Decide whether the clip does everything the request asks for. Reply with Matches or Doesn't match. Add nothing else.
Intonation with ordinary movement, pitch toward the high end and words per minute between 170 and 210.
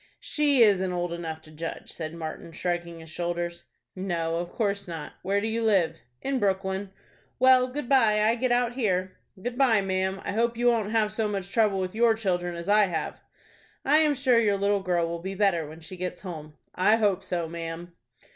Matches